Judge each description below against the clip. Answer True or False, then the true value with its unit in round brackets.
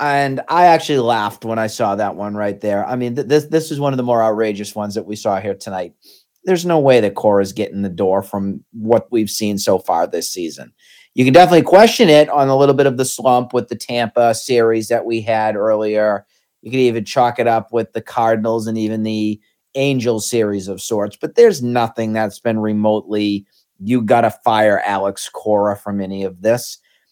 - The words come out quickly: True (210 wpm)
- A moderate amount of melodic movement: True (3.2 semitones)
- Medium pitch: False (115 Hz)